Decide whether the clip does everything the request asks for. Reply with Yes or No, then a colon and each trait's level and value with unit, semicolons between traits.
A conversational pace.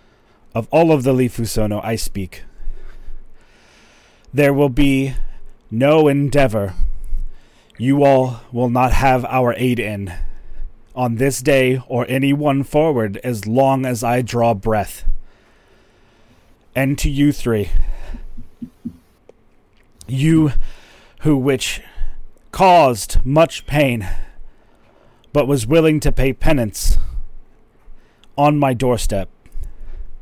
No: slow, 105 wpm